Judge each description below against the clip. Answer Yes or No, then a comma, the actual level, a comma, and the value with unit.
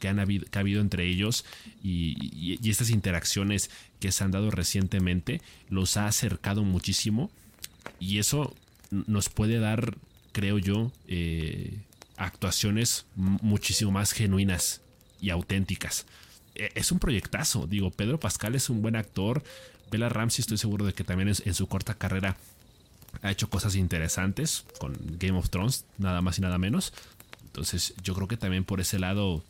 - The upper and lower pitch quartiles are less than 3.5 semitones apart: Yes, narrow, 2.6 semitones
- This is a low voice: Yes, low, 100 Hz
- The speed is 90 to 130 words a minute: No, average, 160 wpm